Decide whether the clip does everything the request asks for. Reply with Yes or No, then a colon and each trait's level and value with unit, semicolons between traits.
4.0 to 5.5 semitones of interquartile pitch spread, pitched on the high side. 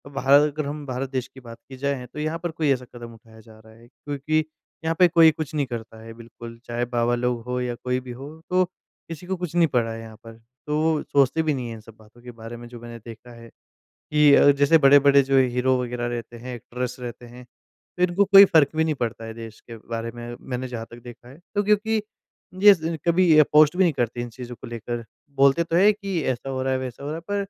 No: average, 4.4 semitones; low, 130 Hz